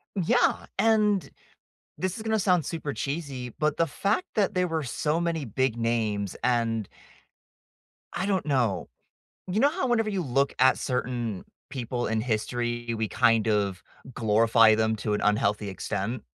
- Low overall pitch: Yes, low, 125 Hz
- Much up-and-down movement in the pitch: Yes, wide, 7.4 semitones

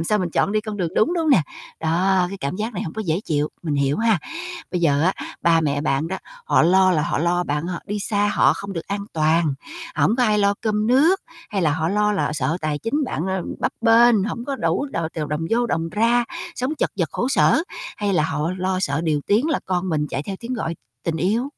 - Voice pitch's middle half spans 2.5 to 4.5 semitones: No, average, 5.2 semitones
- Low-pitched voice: No, high, 190 Hz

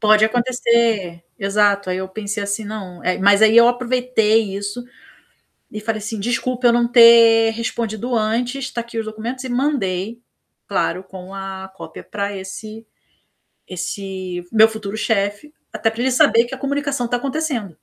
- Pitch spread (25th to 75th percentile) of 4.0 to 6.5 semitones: No, average, 3.1 semitones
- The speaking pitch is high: Yes, high, 220 Hz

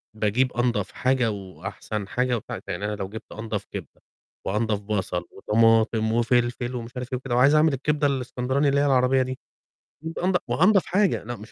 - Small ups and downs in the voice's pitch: No, average, 3.7 semitones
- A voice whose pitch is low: Yes, low, 120 Hz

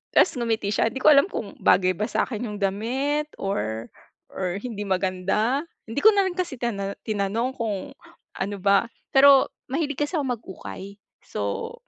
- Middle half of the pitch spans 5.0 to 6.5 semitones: Yes, wide, 5.5 semitones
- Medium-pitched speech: No, high, 220 Hz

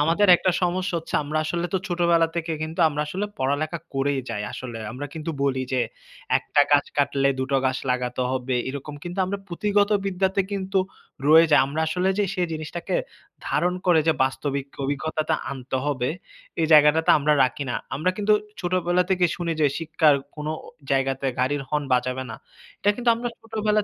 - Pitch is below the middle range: No, medium, 155 Hz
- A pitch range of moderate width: Yes, average, 4.6 semitones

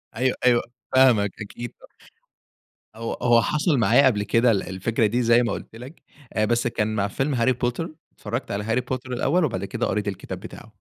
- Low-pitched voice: Yes, low, 120 Hz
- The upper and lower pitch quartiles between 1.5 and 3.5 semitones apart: Yes, average, 2.9 semitones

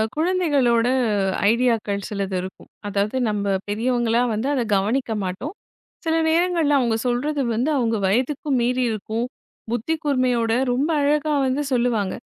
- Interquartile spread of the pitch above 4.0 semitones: Yes, average, 4.5 semitones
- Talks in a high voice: Yes, high, 245 Hz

